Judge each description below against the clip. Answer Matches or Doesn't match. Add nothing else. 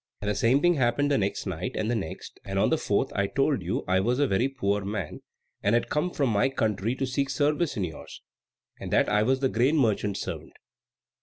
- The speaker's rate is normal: Doesn't match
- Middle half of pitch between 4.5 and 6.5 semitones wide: Matches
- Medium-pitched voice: Doesn't match